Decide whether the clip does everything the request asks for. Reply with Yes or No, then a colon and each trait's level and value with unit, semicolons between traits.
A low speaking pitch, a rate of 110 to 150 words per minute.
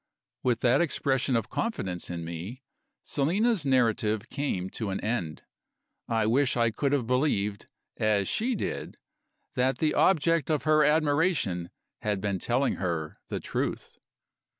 Yes: low, 125 Hz; average, 140 wpm